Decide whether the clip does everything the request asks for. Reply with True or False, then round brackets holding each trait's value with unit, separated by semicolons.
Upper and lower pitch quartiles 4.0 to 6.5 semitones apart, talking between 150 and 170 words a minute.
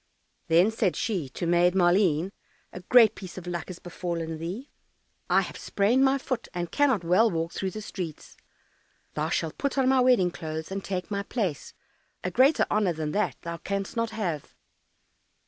False (4.7 semitones; 180 wpm)